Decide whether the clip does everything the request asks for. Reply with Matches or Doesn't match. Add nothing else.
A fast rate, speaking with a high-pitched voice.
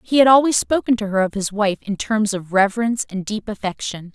Matches